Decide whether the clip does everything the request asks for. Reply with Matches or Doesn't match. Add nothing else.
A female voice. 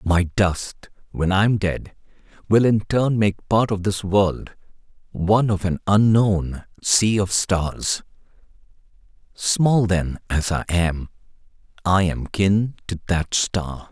Doesn't match